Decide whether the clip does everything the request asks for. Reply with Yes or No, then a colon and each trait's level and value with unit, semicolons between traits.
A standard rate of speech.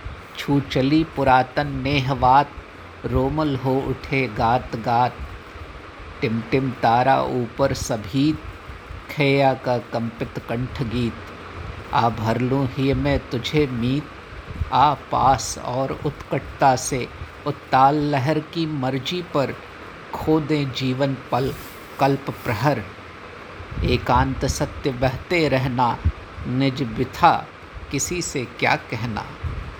No: slow, 100 wpm